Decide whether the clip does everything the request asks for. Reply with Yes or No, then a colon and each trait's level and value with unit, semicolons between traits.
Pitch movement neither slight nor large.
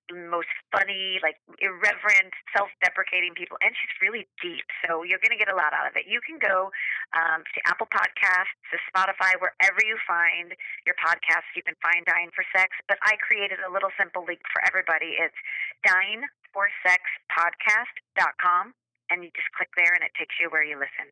No: narrow, 2.1 semitones